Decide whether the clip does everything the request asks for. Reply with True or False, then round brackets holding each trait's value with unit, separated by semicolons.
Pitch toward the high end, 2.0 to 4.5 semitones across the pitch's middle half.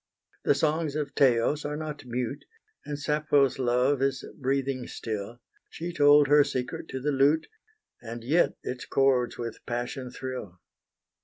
False (135 Hz; 2.9 semitones)